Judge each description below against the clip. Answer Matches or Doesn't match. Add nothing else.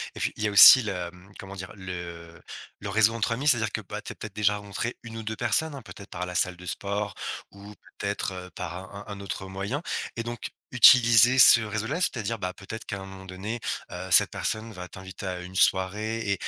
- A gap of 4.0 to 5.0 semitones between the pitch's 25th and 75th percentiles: Doesn't match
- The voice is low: Matches